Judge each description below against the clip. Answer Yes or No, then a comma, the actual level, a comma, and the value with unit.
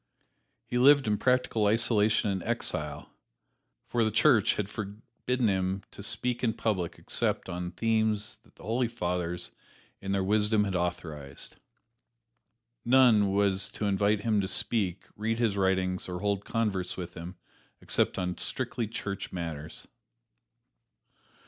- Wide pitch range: No, average, 3.3 semitones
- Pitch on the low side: Yes, low, 100 Hz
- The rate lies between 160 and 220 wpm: No, slow, 135 wpm